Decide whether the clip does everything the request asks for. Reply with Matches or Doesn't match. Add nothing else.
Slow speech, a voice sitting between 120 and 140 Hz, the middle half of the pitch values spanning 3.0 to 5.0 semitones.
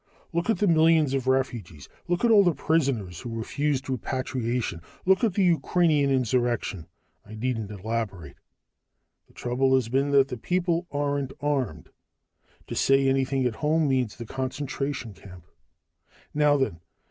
Doesn't match